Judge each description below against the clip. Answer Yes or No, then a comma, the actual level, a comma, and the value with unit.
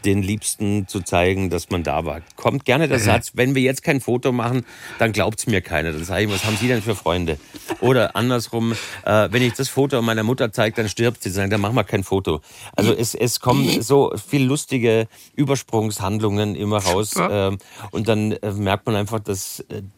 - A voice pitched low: Yes, low, 110 Hz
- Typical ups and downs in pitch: Yes, average, 3.4 semitones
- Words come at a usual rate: No, fast, 205 wpm